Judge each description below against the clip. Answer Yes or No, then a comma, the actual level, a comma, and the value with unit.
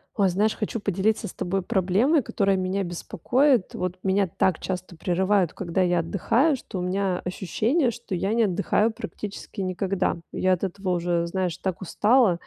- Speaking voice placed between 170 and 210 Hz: Yes, high, 190 Hz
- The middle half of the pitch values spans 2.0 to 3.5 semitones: Yes, average, 2.7 semitones